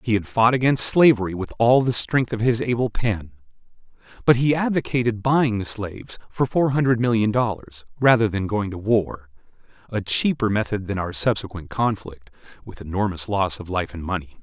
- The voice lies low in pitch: Yes, low, 110 Hz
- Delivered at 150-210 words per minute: Yes, average, 175 wpm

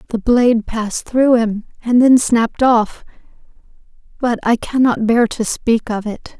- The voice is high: Yes, high, 235 Hz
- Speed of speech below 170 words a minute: Yes, average, 160 wpm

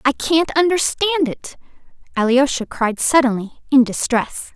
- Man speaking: No, female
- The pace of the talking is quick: No, slow, 120 wpm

